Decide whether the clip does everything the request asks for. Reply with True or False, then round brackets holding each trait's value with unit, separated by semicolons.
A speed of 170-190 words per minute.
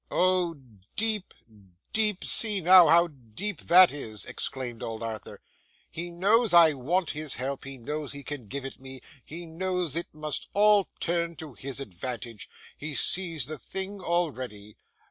False (155 wpm)